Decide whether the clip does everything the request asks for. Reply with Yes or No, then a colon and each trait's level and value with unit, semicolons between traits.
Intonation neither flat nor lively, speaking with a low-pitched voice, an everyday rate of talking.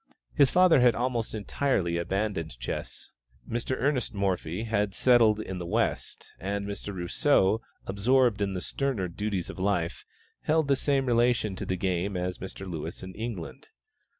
Yes: average, 4.7 semitones; low, 100 Hz; average, 155 wpm